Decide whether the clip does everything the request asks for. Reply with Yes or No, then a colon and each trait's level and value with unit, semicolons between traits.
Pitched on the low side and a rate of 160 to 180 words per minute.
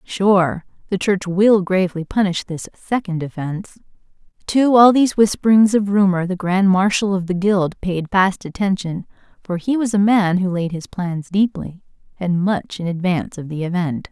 No: high, 190 Hz; average, 175 wpm